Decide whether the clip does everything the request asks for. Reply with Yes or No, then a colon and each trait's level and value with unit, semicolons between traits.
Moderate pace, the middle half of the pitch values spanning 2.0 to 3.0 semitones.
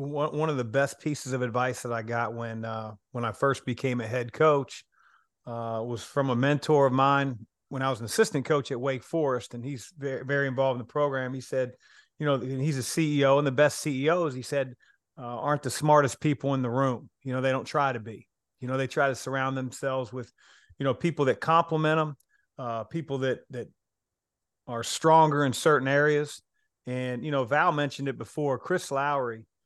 No: fast, 210 wpm; average, 2.7 semitones